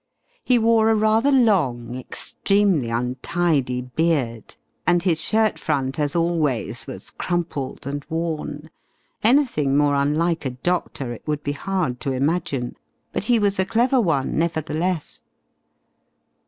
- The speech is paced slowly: Yes, slow, 130 wpm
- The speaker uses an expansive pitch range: Yes, wide, 5.9 semitones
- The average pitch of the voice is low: No, medium, 160 Hz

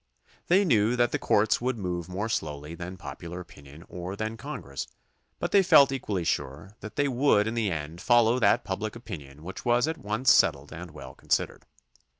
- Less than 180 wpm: No, average, 185 wpm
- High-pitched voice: No, low, 100 Hz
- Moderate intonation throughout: No, wide, 6.9 semitones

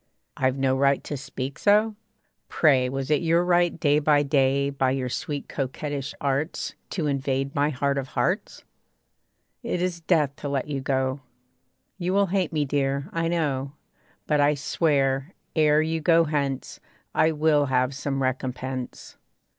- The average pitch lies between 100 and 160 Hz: Yes, medium, 140 Hz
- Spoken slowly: No, average, 155 wpm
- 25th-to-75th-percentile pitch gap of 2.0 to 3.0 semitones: Yes, average, 2.7 semitones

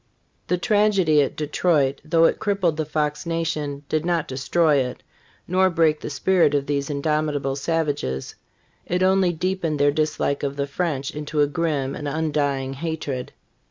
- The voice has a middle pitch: Yes, medium, 150 Hz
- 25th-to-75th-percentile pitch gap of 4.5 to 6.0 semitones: No, average, 2.9 semitones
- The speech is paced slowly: No, average, 160 wpm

